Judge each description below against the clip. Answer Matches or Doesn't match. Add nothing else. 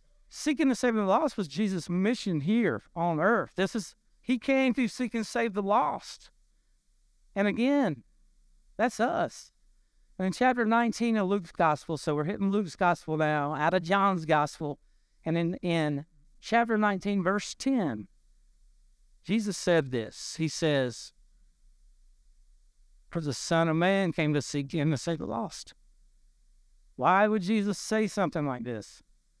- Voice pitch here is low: Doesn't match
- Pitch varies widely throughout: Matches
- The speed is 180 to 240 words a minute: Doesn't match